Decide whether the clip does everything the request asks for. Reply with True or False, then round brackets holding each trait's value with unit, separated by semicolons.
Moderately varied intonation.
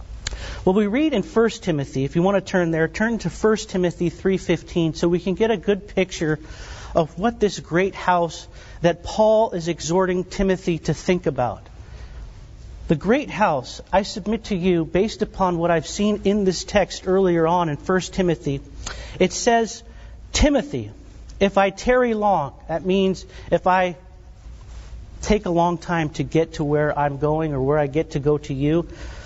True (3.6 semitones)